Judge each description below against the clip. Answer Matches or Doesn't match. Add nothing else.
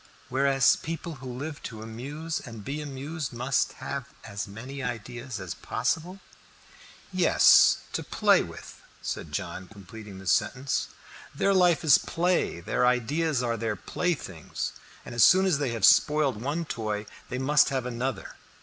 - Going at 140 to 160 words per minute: Matches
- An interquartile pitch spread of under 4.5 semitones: Doesn't match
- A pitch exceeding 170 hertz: Doesn't match